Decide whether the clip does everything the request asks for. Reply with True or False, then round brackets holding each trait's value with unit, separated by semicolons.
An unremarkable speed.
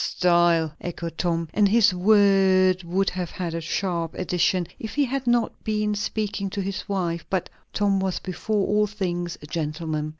True (170 wpm)